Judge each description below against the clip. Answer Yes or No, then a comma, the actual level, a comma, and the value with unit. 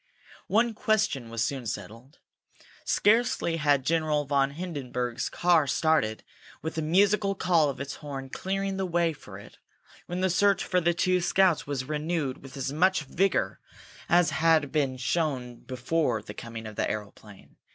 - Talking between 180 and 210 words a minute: No, average, 160 wpm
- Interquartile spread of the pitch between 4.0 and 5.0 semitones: No, wide, 5.4 semitones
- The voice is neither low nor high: Yes, medium, 155 Hz